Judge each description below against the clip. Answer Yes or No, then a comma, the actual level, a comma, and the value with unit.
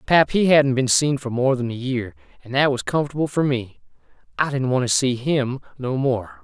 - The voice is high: No, low, 130 Hz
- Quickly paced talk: Yes, fast, 225 wpm